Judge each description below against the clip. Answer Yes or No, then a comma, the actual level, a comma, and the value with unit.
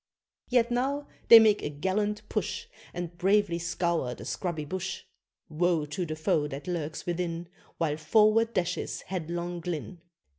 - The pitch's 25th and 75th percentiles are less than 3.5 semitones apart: No, average, 4.4 semitones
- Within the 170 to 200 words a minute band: No, average, 145 wpm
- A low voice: No, medium, 175 Hz